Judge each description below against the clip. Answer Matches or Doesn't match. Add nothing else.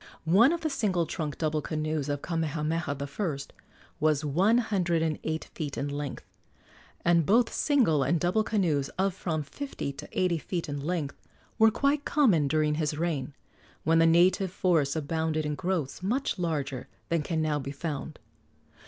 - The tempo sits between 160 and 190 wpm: Matches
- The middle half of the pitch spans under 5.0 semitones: Matches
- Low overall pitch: Doesn't match